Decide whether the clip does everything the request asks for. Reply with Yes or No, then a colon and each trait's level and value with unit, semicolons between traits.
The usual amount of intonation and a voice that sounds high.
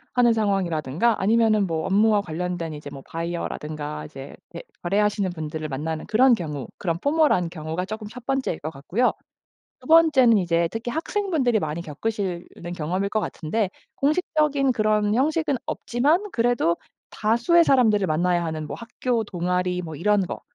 No: wide, 6.4 semitones; high, 200 Hz